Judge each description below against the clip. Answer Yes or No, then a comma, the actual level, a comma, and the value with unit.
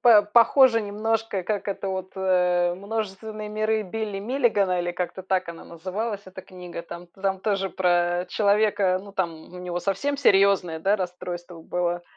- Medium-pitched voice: No, high, 195 Hz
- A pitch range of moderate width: Yes, average, 3.0 semitones